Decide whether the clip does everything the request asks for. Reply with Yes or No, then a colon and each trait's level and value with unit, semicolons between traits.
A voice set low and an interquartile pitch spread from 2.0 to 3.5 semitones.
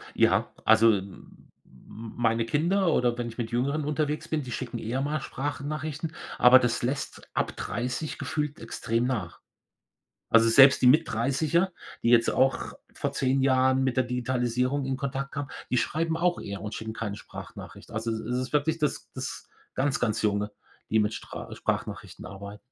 No: low, 130 Hz; average, 4.1 semitones